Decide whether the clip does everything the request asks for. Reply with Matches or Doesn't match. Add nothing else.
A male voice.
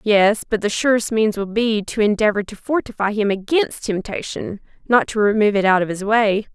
Doesn't match